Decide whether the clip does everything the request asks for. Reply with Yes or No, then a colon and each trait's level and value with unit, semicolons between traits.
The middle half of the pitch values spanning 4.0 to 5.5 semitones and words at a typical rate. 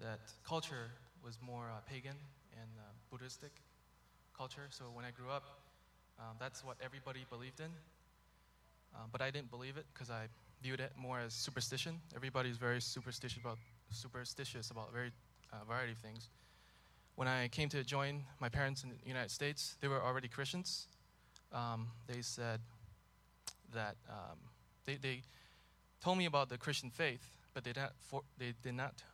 No: average, 3.0 semitones; average, 165 wpm